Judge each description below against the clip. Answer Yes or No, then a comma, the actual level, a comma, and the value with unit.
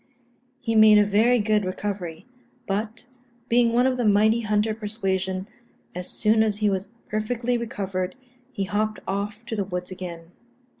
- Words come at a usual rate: Yes, average, 155 wpm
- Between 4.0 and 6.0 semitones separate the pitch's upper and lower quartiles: No, narrow, 2.5 semitones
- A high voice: Yes, high, 210 Hz